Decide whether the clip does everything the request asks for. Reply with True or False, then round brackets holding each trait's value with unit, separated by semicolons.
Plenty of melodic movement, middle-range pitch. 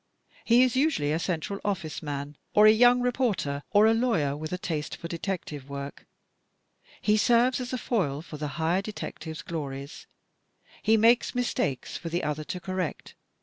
True (7.1 semitones; 180 Hz)